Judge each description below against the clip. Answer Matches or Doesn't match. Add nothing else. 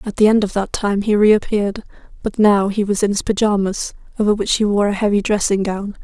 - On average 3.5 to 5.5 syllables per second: Doesn't match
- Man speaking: Doesn't match